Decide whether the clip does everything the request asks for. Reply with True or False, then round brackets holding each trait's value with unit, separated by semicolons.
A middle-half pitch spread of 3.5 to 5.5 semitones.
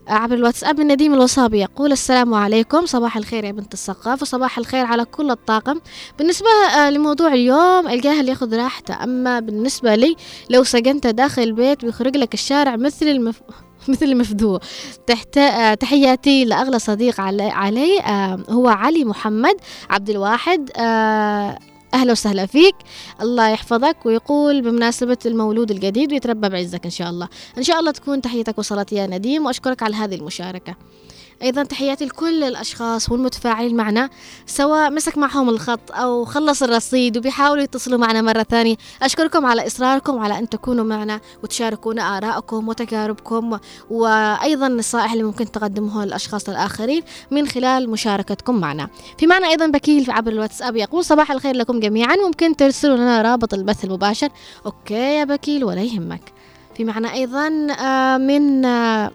True (4.2 semitones)